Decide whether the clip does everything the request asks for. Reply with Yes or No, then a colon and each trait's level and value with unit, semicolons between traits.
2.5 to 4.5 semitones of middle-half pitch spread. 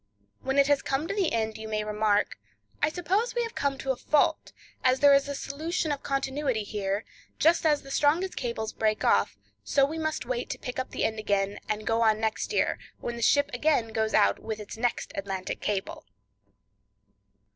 No: average, 5.1 semitones